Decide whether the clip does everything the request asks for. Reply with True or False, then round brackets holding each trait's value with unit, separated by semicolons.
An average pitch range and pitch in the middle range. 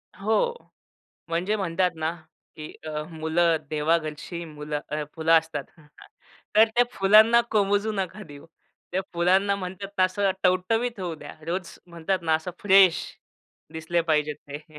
True (3.8 semitones; 175 Hz)